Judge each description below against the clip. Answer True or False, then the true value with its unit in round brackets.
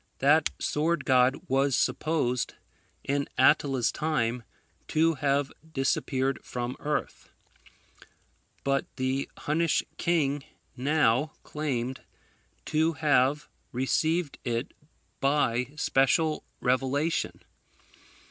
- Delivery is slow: True (85 wpm)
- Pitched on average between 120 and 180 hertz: True (140 Hz)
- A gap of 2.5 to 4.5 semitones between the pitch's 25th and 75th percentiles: True (2.9 semitones)